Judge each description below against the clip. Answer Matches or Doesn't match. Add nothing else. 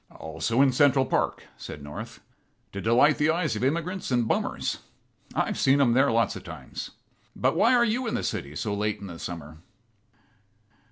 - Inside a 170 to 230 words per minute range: Matches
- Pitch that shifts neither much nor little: Doesn't match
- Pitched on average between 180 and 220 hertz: Doesn't match